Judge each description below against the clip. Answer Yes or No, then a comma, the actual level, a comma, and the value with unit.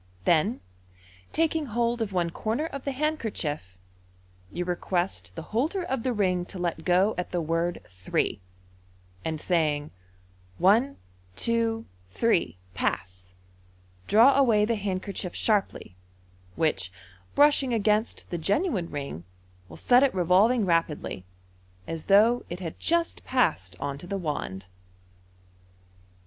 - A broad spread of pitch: Yes, wide, 7.0 semitones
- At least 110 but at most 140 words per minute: Yes, slow, 135 wpm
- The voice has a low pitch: No, medium, 185 Hz